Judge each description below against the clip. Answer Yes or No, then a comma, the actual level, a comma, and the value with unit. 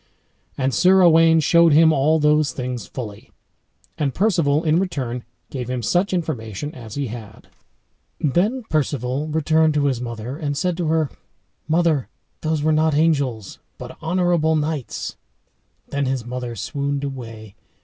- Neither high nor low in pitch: Yes, medium, 145 Hz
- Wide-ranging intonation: No, average, 4.1 semitones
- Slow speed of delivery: No, average, 145 wpm